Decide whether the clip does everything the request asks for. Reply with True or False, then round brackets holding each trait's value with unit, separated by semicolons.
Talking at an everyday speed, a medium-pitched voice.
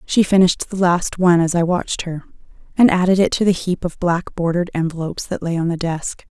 False (230 wpm; 175 Hz)